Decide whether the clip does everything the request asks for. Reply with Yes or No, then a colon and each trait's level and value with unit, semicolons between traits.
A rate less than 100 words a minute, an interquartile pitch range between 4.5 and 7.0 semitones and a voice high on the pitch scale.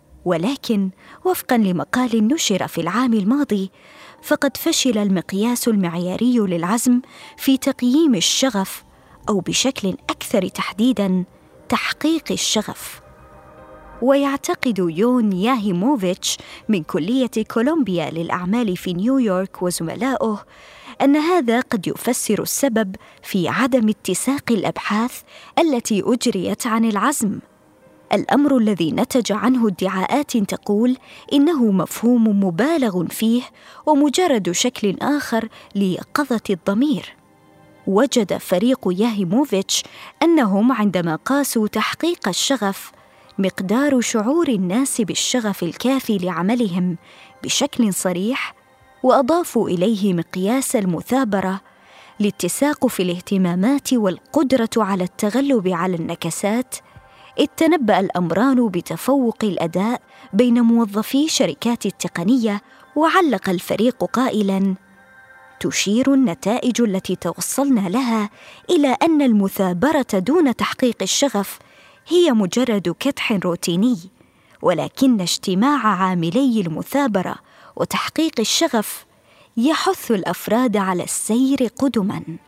Yes: average, 90 wpm; wide, 5.5 semitones; high, 225 Hz